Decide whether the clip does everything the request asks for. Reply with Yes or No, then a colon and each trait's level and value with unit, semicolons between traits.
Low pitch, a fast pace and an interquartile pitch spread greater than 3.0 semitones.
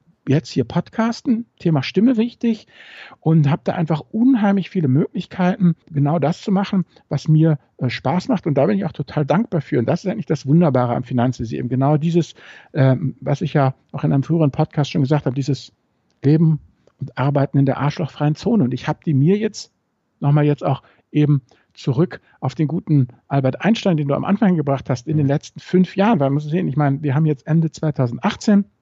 No: medium, 150 Hz; fast, 205 wpm; average, 4.6 semitones